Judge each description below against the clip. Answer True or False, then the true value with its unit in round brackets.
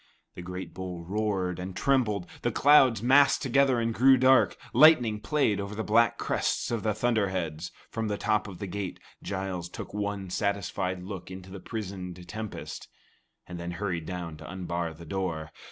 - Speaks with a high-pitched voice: False (100 Hz)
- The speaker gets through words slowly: False (175 wpm)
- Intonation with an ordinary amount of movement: True (3.6 semitones)